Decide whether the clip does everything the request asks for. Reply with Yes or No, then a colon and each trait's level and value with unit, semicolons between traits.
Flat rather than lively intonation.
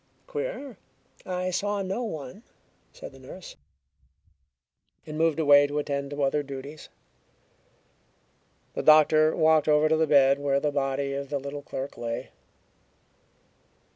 Yes: narrow, 2.3 semitones